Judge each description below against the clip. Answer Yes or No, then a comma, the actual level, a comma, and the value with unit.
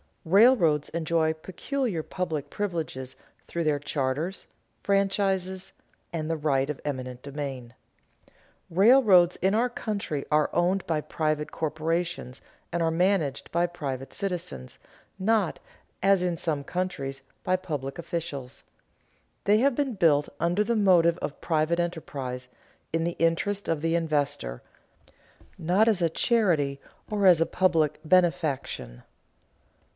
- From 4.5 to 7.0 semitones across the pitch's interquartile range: No, average, 4.1 semitones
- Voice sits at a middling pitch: Yes, medium, 165 Hz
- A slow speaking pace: Yes, slow, 125 wpm